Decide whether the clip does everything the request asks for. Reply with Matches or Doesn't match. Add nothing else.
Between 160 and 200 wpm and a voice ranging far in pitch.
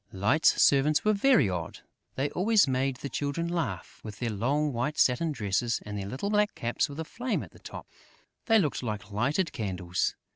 Matches